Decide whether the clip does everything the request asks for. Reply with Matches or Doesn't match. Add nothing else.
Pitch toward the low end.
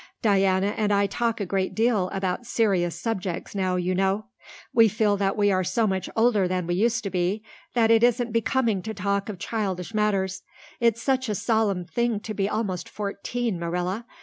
Doesn't match